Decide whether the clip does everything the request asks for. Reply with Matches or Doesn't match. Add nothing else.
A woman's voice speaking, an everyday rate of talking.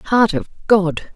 Matches